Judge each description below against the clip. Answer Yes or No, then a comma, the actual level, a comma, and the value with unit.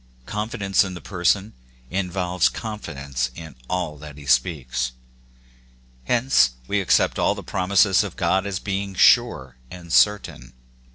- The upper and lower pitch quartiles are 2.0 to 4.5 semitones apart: No, average, 5.3 semitones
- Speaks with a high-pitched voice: No, very low, 90 Hz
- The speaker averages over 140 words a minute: No, slow, 135 wpm